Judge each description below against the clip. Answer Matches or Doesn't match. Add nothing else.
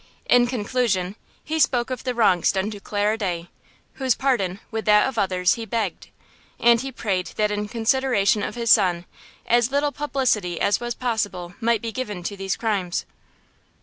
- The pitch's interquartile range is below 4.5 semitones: Matches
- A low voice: Doesn't match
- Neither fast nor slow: Matches